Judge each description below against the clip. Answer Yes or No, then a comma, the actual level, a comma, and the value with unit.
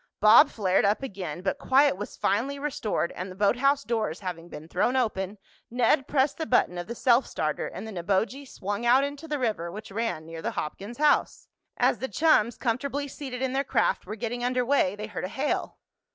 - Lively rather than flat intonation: Yes, wide, 5.7 semitones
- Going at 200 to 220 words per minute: Yes, fast, 205 wpm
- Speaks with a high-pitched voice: Yes, high, 230 Hz